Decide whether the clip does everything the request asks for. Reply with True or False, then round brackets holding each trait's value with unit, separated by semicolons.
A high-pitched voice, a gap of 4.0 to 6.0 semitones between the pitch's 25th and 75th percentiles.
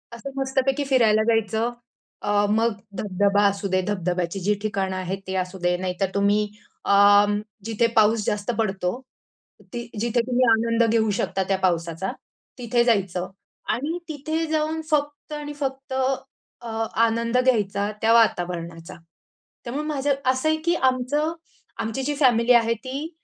True (225 Hz; 4.7 semitones)